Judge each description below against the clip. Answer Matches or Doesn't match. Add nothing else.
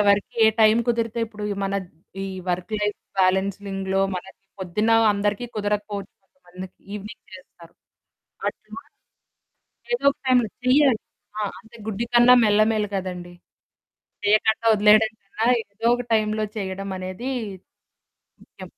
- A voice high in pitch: Matches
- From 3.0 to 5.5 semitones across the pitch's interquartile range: Doesn't match